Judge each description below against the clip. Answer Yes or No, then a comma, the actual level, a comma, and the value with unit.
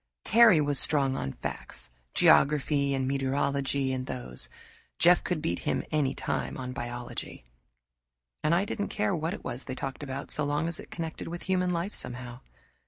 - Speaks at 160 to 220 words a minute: Yes, average, 170 wpm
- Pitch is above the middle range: No, medium, 140 Hz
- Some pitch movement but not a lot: Yes, average, 4.3 semitones